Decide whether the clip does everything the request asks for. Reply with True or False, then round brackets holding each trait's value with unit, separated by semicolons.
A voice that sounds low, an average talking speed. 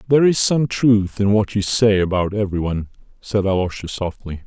True (100 Hz; 190 wpm)